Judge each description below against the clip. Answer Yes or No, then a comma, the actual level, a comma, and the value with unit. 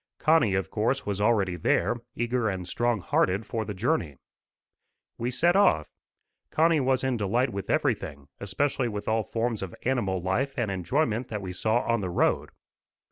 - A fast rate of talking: No, average, 170 wpm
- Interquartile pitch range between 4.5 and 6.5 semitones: Yes, average, 4.8 semitones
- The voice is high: No, low, 110 Hz